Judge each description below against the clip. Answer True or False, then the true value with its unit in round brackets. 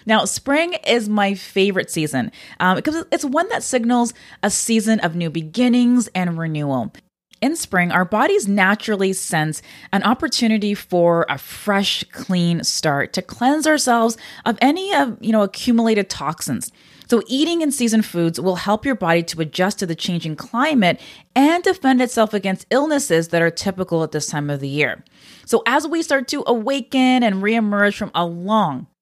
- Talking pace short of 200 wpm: True (170 wpm)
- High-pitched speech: True (210 Hz)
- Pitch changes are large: True (5.8 semitones)